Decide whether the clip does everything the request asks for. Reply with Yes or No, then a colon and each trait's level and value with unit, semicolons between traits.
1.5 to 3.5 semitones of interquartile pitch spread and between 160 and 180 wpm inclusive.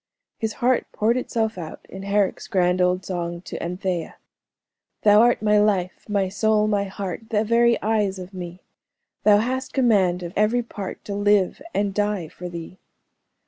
Yes: average, 3.1 semitones; average, 165 wpm